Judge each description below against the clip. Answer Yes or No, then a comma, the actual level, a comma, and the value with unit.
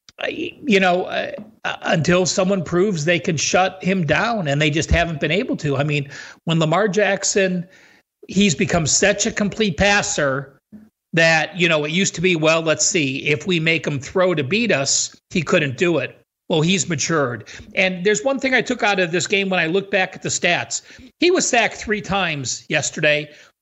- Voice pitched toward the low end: No, medium, 185 Hz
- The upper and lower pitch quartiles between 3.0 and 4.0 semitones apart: No, average, 4.4 semitones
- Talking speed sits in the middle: Yes, average, 195 wpm